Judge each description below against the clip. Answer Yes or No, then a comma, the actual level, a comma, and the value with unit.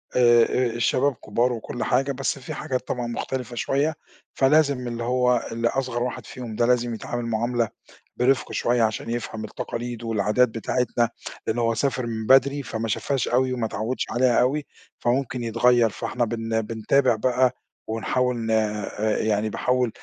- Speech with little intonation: Yes, narrow, 2.0 semitones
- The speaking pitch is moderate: No, low, 120 Hz